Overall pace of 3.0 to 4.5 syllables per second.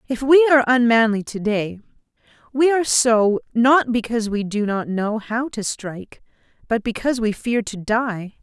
No: 5.0 syllables/s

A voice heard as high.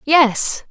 Yes: very high, 265 Hz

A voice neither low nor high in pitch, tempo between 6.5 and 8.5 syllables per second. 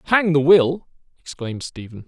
No: medium, 150 Hz; 5.2 syllables/s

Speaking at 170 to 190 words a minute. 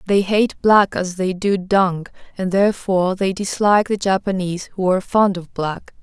Yes: average, 180 wpm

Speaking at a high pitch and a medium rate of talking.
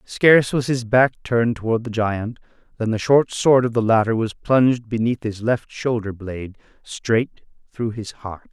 No: low, 115 Hz; average, 185 wpm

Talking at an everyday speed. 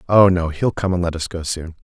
No: fast, 290 wpm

